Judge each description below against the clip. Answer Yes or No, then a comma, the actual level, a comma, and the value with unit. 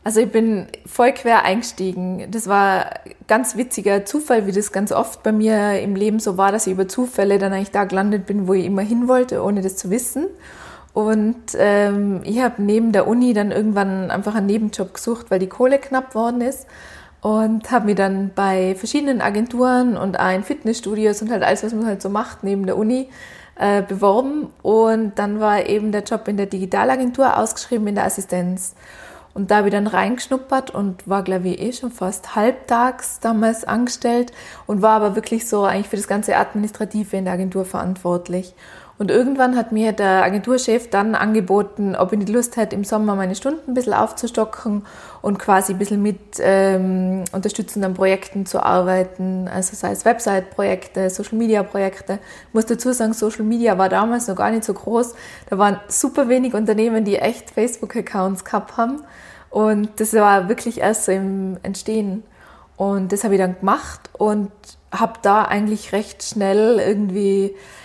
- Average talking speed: Yes, average, 180 wpm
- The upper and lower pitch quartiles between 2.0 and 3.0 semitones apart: Yes, average, 2.7 semitones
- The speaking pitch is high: Yes, high, 210 Hz